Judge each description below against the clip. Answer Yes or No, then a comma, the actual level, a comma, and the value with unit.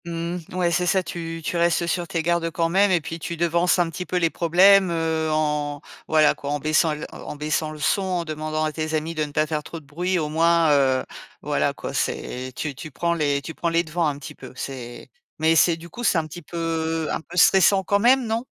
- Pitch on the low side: No, medium, 165 Hz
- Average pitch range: No, narrow, 2.0 semitones